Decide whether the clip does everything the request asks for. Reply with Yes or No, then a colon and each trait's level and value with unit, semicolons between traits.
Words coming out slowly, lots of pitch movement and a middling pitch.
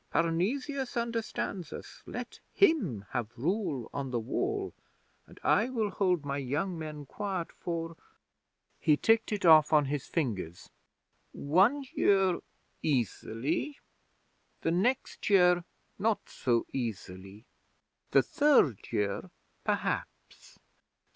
Yes: slow, 110 wpm; wide, 8.2 semitones; medium, 165 Hz